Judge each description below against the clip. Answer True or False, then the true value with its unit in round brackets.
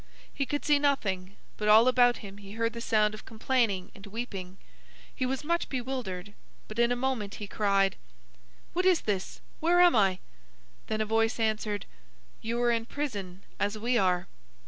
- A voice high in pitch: True (225 Hz)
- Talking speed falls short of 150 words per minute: False (175 wpm)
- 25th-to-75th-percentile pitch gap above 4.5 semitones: False (4.0 semitones)